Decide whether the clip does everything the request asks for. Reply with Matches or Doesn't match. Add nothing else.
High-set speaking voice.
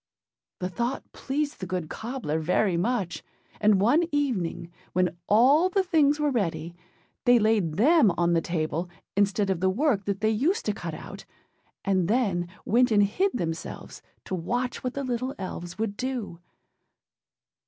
Matches